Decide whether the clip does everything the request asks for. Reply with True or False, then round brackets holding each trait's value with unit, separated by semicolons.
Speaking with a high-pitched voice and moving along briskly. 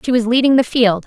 True (240 Hz; 280 wpm)